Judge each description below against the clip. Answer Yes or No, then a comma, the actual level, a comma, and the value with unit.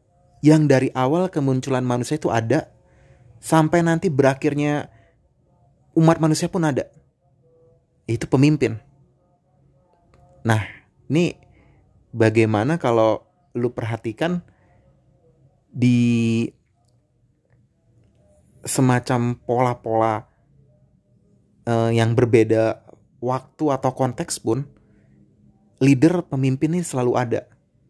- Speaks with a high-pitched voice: No, low, 130 Hz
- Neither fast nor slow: No, slow, 75 wpm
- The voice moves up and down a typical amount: Yes, average, 4.1 semitones